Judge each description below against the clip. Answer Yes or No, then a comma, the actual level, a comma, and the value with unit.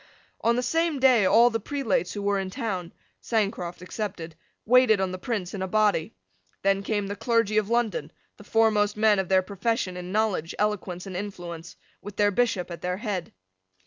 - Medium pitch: No, high, 205 Hz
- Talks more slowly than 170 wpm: No, average, 185 wpm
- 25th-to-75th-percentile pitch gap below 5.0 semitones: Yes, average, 3.3 semitones